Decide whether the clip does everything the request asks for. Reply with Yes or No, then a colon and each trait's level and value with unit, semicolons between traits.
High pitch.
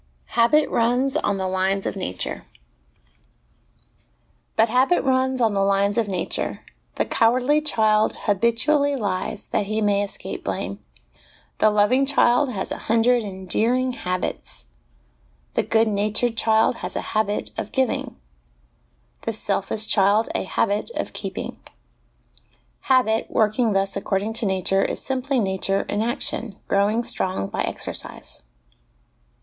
Yes: high, 220 Hz